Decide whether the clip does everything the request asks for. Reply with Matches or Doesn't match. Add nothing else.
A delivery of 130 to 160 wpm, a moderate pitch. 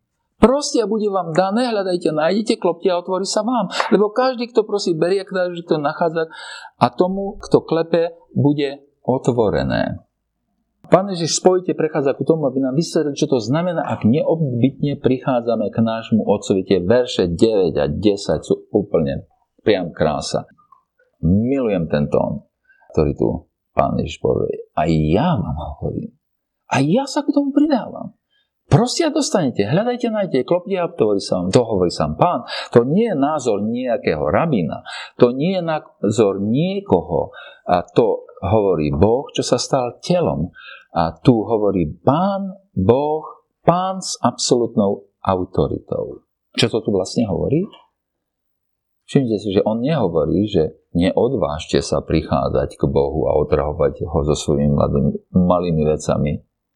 Matches